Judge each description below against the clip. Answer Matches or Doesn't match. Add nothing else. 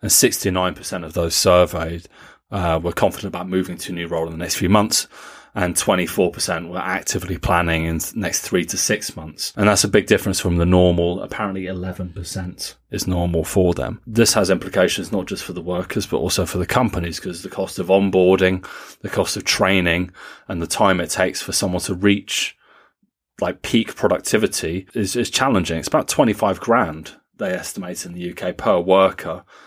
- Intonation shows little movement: Matches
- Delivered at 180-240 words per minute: Matches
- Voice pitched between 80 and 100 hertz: Matches